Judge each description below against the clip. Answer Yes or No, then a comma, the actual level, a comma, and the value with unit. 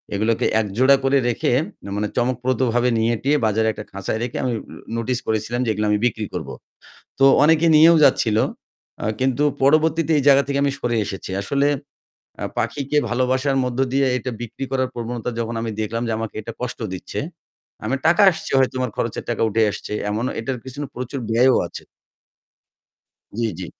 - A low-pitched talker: Yes, low, 125 Hz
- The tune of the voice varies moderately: Yes, average, 3.3 semitones